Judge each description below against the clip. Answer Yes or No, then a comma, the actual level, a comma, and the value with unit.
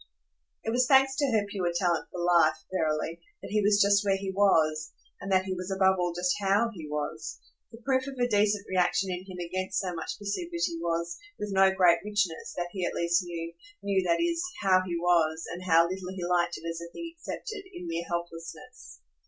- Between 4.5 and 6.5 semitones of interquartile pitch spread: No, average, 3.1 semitones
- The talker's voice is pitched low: No, medium, 185 Hz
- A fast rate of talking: Yes, fast, 210 wpm